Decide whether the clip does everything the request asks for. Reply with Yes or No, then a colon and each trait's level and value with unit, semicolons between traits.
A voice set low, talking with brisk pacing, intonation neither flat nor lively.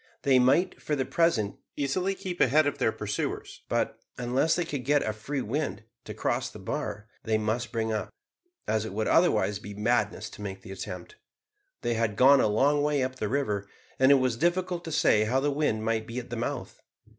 Yes: low, 125 Hz; fast, 210 wpm; average, 5.0 semitones